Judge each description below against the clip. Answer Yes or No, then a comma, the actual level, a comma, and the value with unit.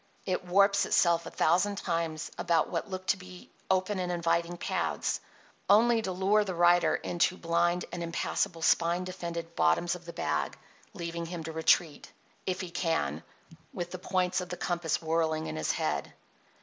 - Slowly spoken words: No, average, 170 wpm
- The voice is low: No, medium, 175 Hz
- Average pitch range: No, narrow, 1.7 semitones